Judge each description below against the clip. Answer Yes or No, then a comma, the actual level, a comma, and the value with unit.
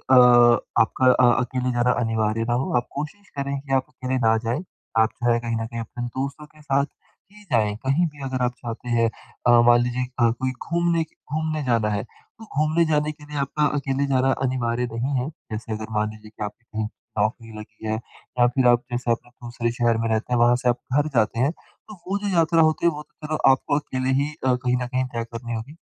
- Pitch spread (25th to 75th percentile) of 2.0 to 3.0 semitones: No, average, 3.6 semitones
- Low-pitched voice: Yes, low, 125 Hz